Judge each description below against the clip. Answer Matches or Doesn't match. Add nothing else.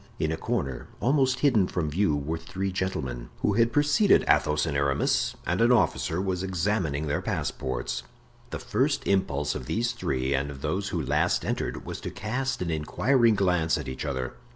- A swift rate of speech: Doesn't match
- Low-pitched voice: Matches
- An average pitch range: Doesn't match